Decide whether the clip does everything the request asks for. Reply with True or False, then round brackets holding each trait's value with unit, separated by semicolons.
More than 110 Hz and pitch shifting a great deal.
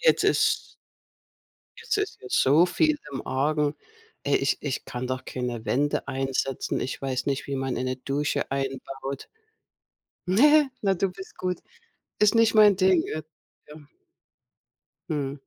True (140 Hz; 5.9 semitones)